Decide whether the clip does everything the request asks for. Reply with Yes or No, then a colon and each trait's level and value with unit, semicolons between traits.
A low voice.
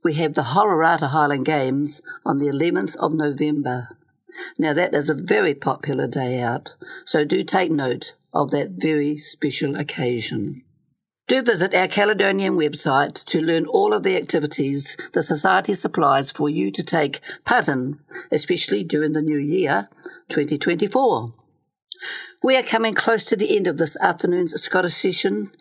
No: medium, 155 Hz